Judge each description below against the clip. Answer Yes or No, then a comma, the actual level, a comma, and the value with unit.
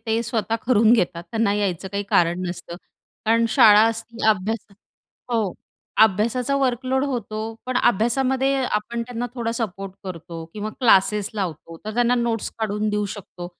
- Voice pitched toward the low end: No, high, 220 Hz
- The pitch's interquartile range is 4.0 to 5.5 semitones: No, average, 3.2 semitones